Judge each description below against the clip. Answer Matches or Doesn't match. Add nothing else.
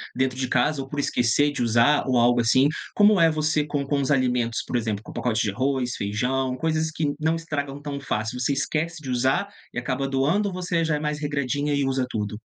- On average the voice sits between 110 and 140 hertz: Matches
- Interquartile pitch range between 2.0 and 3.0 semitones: Doesn't match